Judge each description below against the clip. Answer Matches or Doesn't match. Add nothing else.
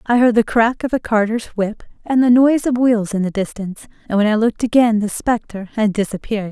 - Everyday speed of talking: Doesn't match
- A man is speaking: Doesn't match